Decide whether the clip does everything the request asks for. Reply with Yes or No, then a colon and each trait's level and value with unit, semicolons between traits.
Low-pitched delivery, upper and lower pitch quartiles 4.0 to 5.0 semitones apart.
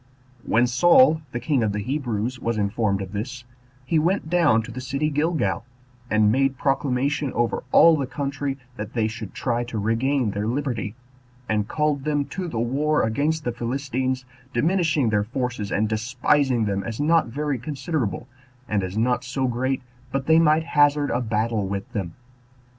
Yes: low, 125 Hz; average, 4.7 semitones